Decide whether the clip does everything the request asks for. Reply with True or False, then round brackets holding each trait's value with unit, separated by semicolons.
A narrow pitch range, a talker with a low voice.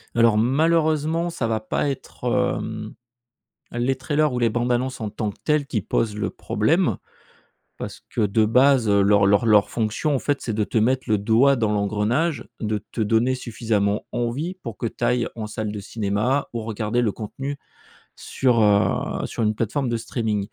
False (3.5 semitones; 115 Hz)